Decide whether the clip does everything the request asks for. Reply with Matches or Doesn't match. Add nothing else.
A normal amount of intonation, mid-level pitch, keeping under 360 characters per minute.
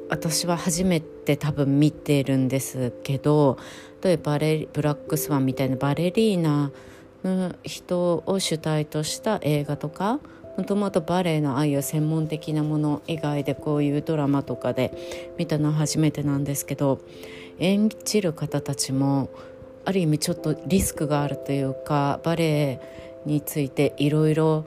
Matches